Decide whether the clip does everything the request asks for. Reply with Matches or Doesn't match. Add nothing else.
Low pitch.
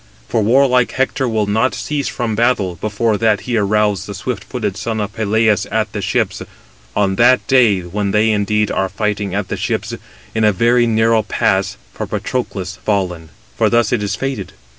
Matches